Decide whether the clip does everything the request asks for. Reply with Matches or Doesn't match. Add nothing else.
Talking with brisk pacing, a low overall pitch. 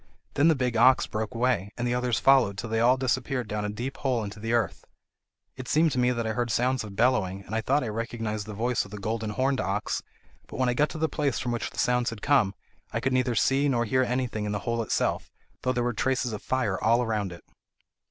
Matches